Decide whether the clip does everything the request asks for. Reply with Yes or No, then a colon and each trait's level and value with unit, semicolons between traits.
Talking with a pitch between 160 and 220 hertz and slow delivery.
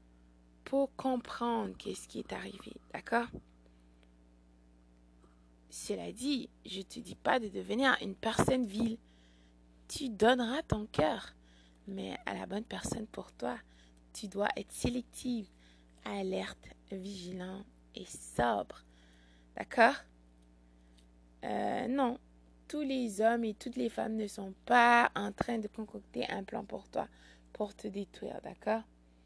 Yes: medium, 185 Hz; slow, 130 wpm